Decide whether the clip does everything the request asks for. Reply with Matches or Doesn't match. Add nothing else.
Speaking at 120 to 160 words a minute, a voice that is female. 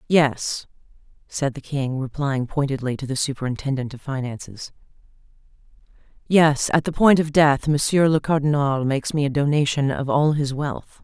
Matches